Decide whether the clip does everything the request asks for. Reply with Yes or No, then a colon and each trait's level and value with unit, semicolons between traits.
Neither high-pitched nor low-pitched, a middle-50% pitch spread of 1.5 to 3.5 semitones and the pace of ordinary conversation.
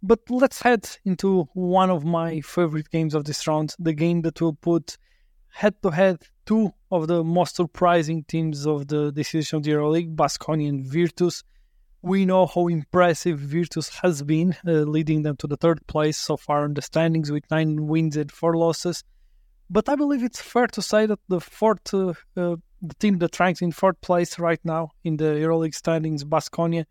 Yes: medium, 165 Hz; average, 2.7 semitones; average, 190 wpm